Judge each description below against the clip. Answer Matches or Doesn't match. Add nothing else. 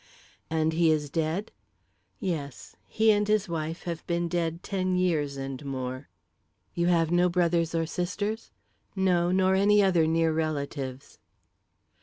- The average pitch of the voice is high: Doesn't match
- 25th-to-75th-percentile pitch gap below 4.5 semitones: Matches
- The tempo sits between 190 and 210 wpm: Doesn't match